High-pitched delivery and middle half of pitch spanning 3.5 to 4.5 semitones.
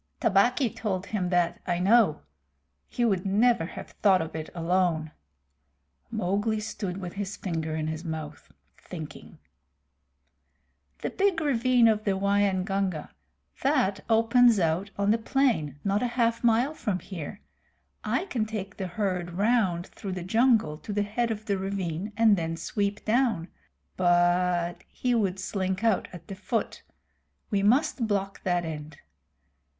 Yes: high, 195 Hz; average, 4.1 semitones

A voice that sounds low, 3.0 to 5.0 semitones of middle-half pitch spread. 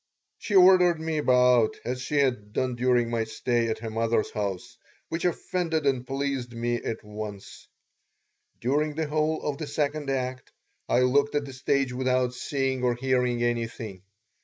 Yes: low, 125 Hz; average, 3.3 semitones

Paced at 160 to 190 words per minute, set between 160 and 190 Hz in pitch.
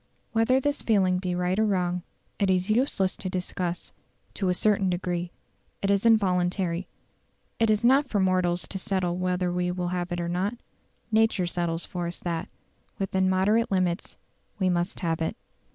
Yes: average, 170 wpm; medium, 185 Hz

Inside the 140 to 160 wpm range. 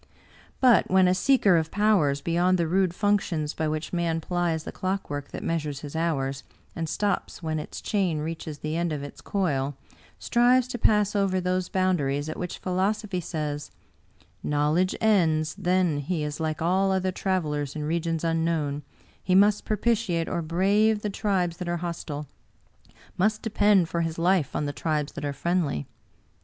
No: average, 175 wpm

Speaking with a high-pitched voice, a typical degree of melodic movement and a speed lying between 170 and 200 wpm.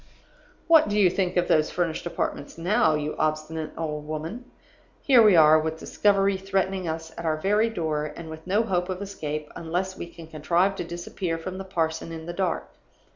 No: medium, 170 Hz; average, 3.3 semitones; average, 190 wpm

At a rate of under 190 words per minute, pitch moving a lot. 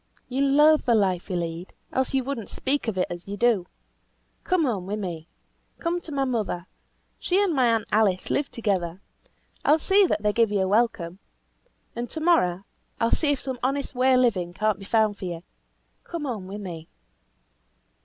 No: fast, 205 wpm; wide, 6.5 semitones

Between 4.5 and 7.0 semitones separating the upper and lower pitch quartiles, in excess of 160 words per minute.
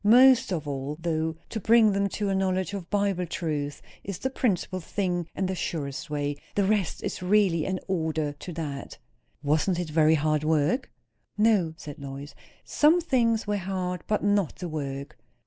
Yes: average, 4.9 semitones; average, 175 wpm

